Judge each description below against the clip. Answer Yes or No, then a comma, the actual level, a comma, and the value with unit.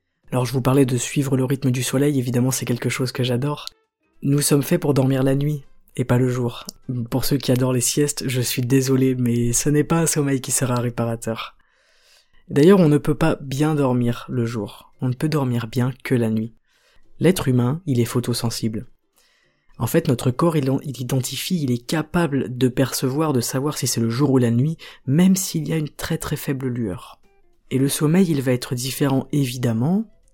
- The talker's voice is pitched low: Yes, low, 130 Hz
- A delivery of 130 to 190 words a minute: No, average, 210 wpm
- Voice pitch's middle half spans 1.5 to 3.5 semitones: Yes, average, 3.1 semitones